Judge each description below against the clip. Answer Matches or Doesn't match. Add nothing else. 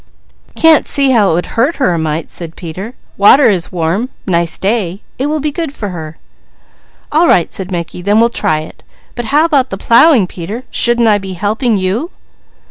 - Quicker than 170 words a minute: Matches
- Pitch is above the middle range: Matches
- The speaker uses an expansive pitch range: Matches